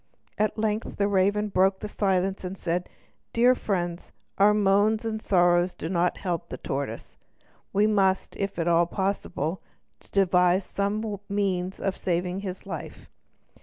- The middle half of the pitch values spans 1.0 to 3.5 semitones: Yes, narrow, 2.4 semitones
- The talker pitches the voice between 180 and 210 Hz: Yes, high, 190 Hz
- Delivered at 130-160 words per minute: Yes, average, 155 wpm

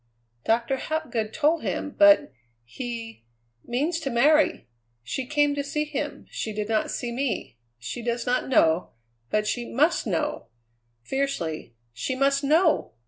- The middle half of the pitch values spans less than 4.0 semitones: No, average, 4.8 semitones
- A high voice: Yes, very high, 255 Hz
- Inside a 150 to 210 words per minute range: No, average, 140 wpm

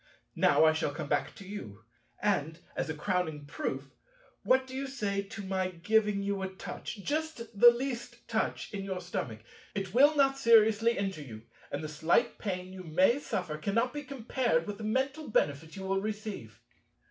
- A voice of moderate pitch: No, high, 200 Hz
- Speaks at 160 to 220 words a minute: Yes, average, 180 wpm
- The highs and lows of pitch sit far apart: Yes, wide, 5.9 semitones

